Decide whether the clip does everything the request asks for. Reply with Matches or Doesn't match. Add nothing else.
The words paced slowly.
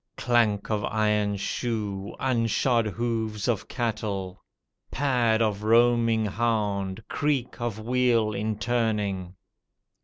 Matches